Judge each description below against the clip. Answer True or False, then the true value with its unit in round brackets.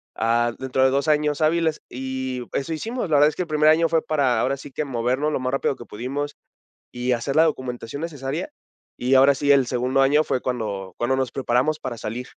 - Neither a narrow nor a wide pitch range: True (3.3 semitones)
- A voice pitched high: False (135 Hz)